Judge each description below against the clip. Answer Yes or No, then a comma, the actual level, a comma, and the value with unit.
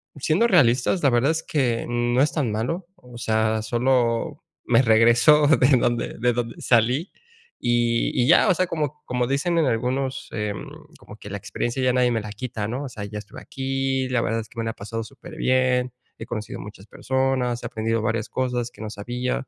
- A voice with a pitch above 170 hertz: No, low, 125 Hz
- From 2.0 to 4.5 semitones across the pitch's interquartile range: Yes, average, 2.7 semitones